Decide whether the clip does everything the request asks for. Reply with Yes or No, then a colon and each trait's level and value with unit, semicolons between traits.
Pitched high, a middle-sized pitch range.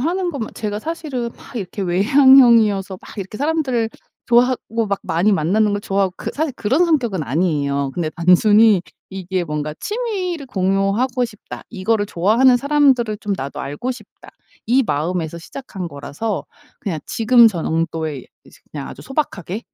No: high, 210 Hz; wide, 5.9 semitones